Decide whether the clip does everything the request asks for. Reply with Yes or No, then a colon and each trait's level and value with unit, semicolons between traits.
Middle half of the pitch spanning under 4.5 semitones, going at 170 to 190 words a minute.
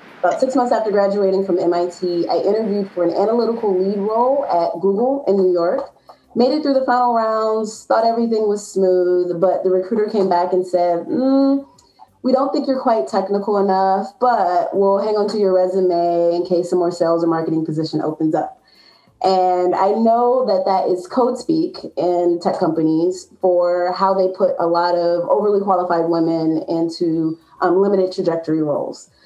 Yes: average, 3.8 semitones; average, 175 wpm